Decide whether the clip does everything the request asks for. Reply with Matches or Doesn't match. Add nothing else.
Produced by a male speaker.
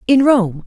Doesn't match